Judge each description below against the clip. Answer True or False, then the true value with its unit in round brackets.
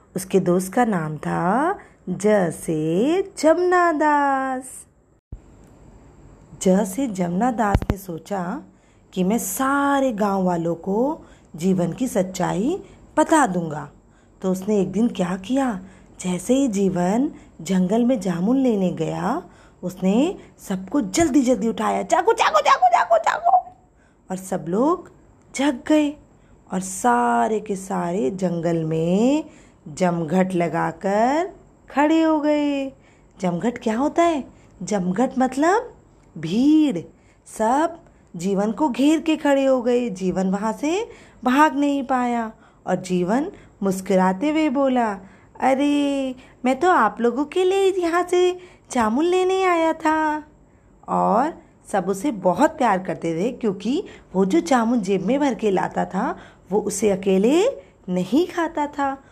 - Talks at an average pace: True (125 wpm)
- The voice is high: True (240 Hz)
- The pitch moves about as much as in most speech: False (7.9 semitones)